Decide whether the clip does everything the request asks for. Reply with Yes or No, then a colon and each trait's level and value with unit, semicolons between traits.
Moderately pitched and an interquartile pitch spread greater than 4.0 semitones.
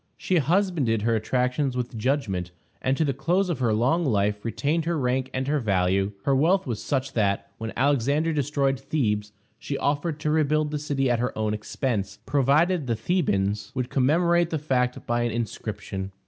No: low, 130 Hz; average, 5.1 semitones